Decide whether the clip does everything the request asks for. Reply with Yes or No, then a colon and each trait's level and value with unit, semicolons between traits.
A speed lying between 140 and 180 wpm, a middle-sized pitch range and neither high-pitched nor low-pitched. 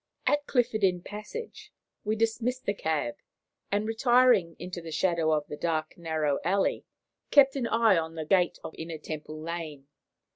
No: average, 160 wpm; wide, 5.9 semitones; medium, 180 Hz